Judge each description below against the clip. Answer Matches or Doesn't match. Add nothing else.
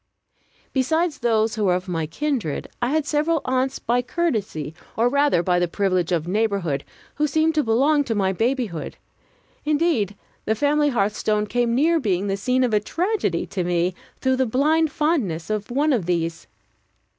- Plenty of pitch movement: Matches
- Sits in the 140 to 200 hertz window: Doesn't match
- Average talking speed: Matches